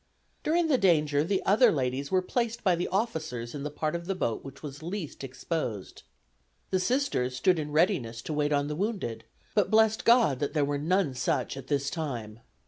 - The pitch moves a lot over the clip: Yes, wide, 6.0 semitones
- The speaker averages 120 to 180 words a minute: No, average, 195 wpm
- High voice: No, medium, 155 Hz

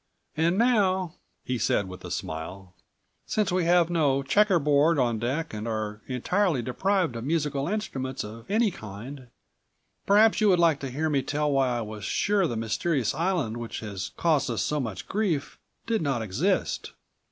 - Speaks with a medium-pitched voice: Yes, medium, 145 Hz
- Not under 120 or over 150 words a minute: No, average, 175 wpm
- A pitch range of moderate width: No, wide, 7.3 semitones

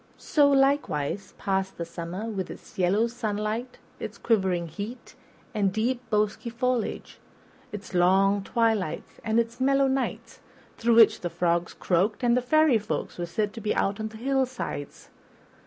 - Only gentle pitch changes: No, average, 4.1 semitones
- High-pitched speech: Yes, high, 220 Hz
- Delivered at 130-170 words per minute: Yes, average, 150 wpm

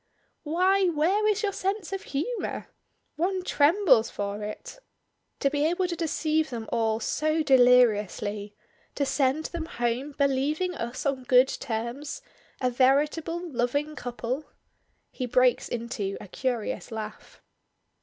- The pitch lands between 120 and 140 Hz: No, very high, 275 Hz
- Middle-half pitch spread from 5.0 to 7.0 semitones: Yes, wide, 5.6 semitones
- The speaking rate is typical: No, slow, 130 wpm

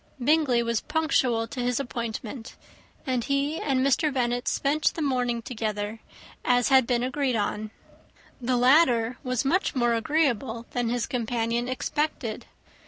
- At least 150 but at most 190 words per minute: No, average, 140 wpm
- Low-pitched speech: No, high, 245 Hz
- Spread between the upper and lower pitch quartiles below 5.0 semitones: Yes, average, 2.9 semitones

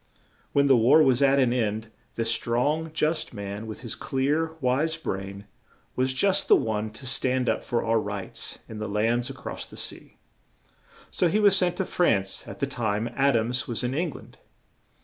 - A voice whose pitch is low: Yes, low, 125 Hz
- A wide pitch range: No, average, 4.6 semitones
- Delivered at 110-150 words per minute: No, average, 190 wpm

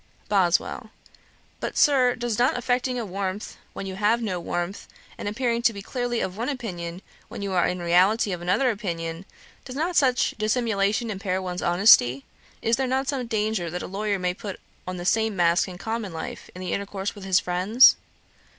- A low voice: No, high, 200 Hz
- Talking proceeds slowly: No, average, 190 wpm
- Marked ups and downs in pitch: No, average, 4.6 semitones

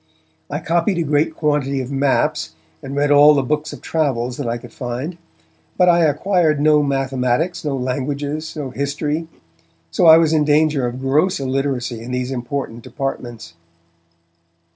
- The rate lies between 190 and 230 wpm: No, average, 165 wpm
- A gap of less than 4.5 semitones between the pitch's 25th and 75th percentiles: Yes, average, 3.1 semitones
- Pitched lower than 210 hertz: Yes, medium, 140 Hz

